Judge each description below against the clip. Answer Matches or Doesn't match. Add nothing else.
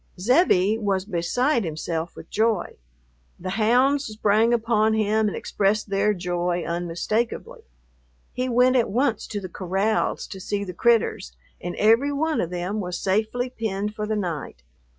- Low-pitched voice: Doesn't match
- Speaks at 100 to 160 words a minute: Matches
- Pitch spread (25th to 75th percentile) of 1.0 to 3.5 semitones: Doesn't match